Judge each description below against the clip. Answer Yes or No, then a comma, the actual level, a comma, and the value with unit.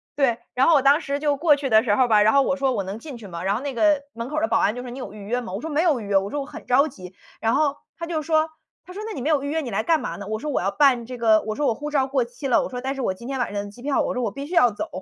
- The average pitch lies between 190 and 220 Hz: No, very high, 265 Hz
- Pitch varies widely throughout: No, average, 4.8 semitones